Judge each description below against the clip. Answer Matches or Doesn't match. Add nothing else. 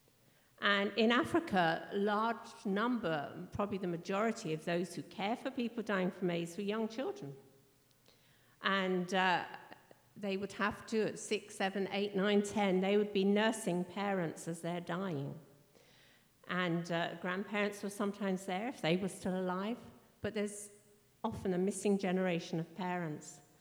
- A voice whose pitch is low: Doesn't match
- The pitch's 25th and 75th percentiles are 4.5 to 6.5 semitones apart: Doesn't match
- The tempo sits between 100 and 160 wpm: Matches